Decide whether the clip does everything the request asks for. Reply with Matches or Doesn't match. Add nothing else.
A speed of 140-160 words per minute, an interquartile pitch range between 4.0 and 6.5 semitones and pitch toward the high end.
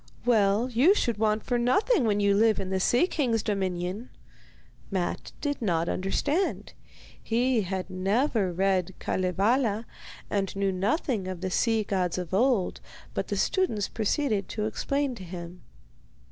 Matches